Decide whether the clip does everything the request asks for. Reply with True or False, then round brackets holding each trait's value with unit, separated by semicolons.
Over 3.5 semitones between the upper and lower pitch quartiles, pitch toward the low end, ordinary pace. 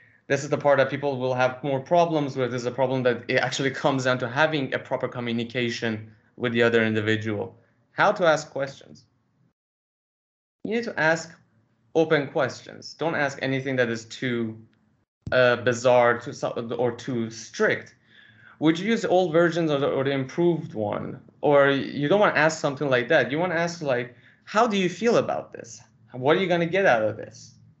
True (4.6 semitones; 130 Hz; 195 wpm)